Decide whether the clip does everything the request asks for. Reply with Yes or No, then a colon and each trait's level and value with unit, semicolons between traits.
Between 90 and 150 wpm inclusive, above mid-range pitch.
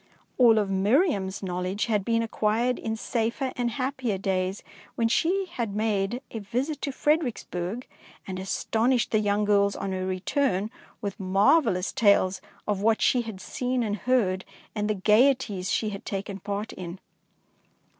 No: average, 160 wpm; high, 215 Hz